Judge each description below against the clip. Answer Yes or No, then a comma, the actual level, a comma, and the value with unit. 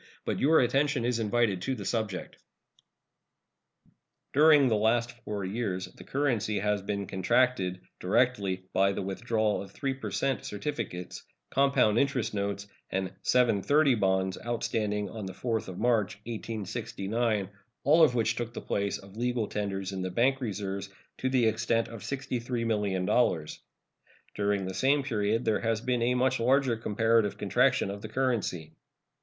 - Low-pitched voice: Yes, low, 110 Hz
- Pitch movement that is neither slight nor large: Yes, average, 3.8 semitones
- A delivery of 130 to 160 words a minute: Yes, average, 150 wpm